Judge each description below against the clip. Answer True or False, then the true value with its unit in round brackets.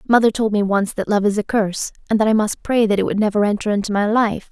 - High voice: True (210 Hz)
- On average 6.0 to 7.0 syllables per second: True (6.5 syllables/s)